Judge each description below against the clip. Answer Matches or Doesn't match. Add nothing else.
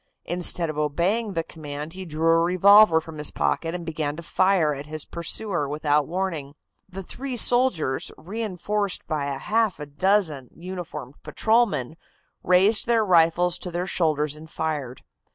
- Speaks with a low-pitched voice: Doesn't match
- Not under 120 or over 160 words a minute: Matches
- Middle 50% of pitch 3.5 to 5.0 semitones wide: Matches